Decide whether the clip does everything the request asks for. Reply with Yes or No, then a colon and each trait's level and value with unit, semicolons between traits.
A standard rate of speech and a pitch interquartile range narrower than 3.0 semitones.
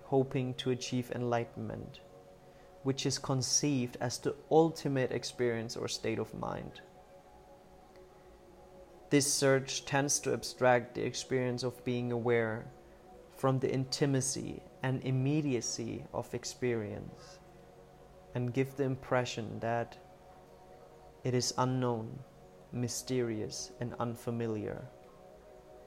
No: slow, 100 wpm; narrow, 2.6 semitones